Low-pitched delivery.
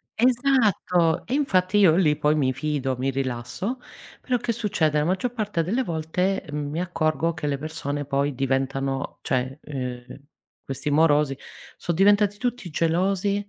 No: medium, 160 Hz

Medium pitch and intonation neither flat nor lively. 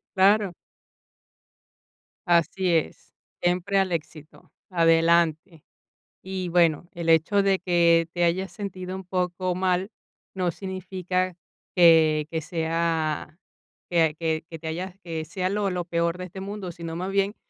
No: medium, 175 Hz; narrow, 2.2 semitones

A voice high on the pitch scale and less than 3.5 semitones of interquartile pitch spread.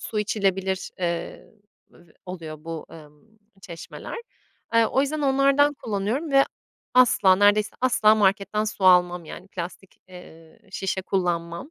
No: high, 195 Hz; average, 4.0 semitones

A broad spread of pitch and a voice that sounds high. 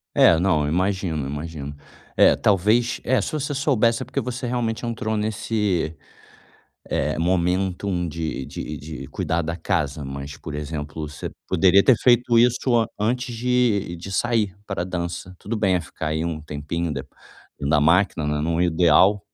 No: wide, 6.2 semitones; very low, 90 Hz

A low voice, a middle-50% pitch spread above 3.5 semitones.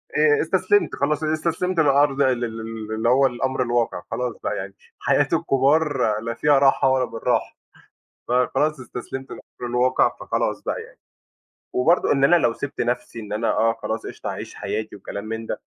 Yes: low, 130 Hz; average, 3.9 semitones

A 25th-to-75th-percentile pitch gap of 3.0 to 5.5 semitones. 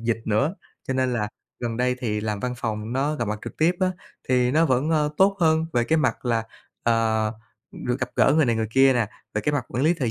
Yes: average, 4.7 semitones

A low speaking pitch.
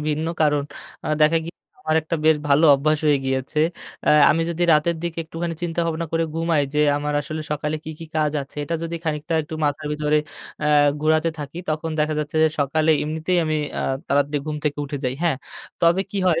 No: medium, 155 Hz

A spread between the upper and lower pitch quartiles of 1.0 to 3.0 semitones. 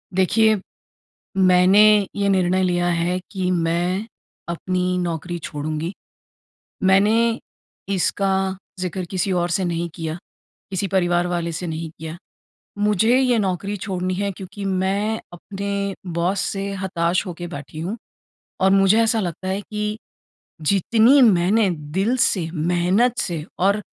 Yes: narrow, 2.5 semitones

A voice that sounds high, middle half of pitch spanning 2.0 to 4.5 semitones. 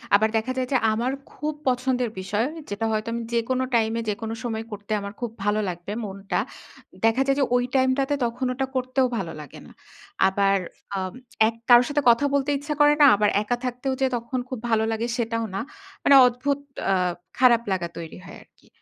Yes: high, 235 Hz; average, 3.6 semitones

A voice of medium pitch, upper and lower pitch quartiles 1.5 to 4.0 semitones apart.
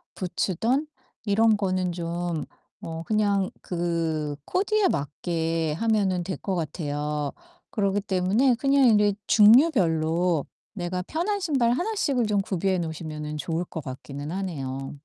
No: medium, 180 Hz; average, 5.1 semitones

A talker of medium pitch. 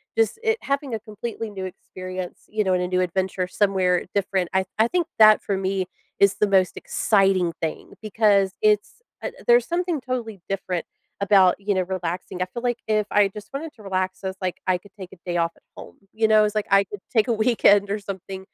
No: high, 200 Hz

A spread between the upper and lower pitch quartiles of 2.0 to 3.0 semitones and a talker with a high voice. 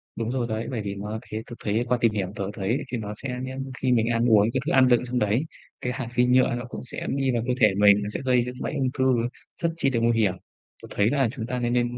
No: narrow, 2.6 semitones; low, 120 Hz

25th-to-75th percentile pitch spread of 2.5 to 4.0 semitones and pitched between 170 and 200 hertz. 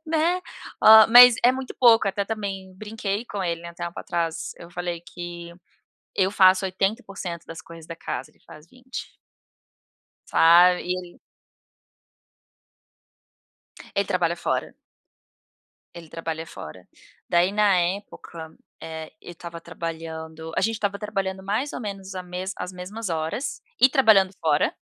Yes: average, 3.5 semitones; medium, 185 Hz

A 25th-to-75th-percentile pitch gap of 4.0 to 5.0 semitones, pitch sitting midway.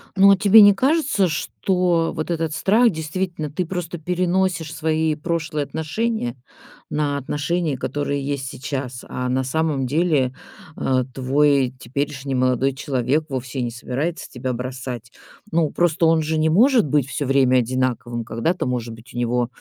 Yes: average, 4.7 semitones; medium, 145 Hz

